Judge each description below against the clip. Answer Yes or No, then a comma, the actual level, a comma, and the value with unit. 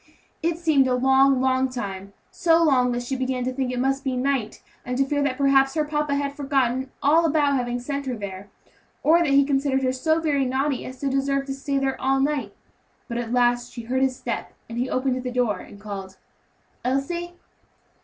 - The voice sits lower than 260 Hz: No, very high, 265 Hz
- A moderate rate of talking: No, fast, 215 wpm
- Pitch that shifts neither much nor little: No, narrow, 2.1 semitones